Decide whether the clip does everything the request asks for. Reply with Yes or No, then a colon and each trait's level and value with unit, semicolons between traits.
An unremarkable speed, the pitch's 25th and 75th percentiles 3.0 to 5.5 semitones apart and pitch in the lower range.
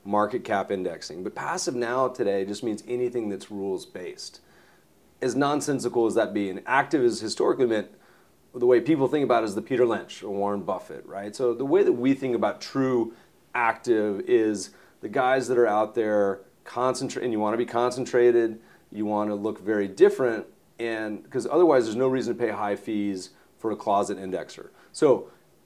Yes: average, 185 wpm; average, 4.0 semitones; low, 115 Hz